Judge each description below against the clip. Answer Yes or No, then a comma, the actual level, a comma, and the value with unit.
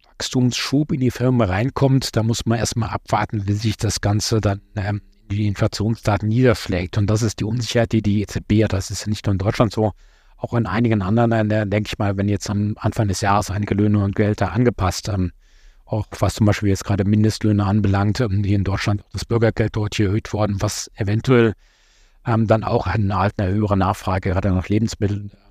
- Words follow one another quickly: Yes, fast, 210 wpm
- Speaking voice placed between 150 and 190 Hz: No, low, 105 Hz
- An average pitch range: No, narrow, 1.9 semitones